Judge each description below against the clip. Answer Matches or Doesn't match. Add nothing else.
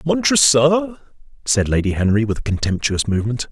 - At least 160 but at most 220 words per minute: Doesn't match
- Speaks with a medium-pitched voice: Doesn't match